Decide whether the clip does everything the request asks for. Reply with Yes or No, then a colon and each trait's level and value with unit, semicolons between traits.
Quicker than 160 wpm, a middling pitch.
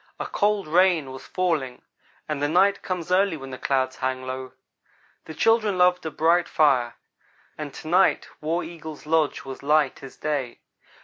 Yes: average, 170 wpm; medium, 155 Hz